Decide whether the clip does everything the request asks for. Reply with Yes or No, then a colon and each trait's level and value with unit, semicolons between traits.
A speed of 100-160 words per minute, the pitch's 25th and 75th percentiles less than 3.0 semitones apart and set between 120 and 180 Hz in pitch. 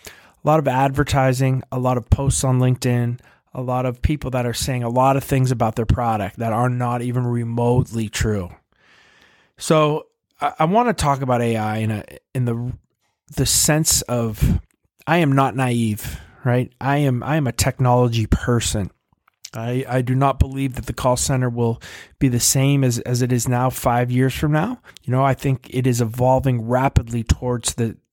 No: average, 190 wpm; narrow, 2.4 semitones; low, 125 Hz